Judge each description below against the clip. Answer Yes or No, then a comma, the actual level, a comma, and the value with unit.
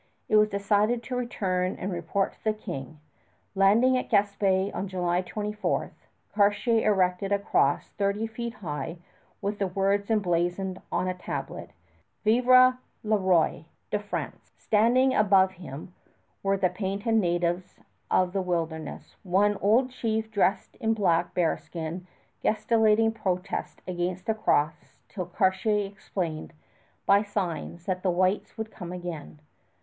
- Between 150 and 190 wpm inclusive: No, slow, 135 wpm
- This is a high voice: Yes, high, 195 Hz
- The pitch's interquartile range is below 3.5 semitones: Yes, average, 3.0 semitones